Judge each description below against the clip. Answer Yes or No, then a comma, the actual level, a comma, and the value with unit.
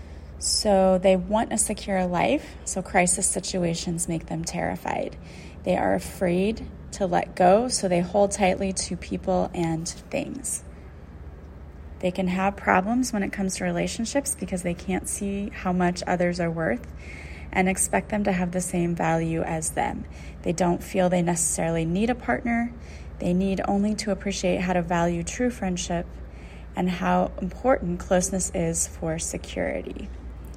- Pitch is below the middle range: No, medium, 180 Hz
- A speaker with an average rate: Yes, average, 155 wpm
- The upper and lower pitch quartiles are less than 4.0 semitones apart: Yes, average, 2.9 semitones